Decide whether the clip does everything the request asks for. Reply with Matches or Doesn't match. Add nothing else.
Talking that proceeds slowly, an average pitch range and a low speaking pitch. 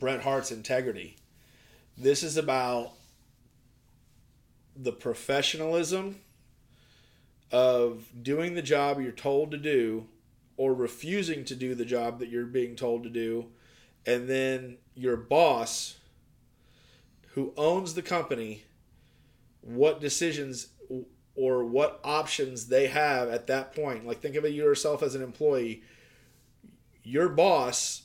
Matches